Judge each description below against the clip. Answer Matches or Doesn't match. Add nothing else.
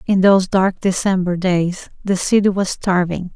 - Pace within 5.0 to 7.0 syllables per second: Doesn't match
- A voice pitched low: Doesn't match